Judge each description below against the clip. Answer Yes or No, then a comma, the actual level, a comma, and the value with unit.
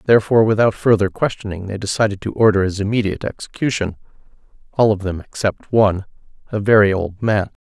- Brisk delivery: No, average, 150 wpm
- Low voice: Yes, low, 105 Hz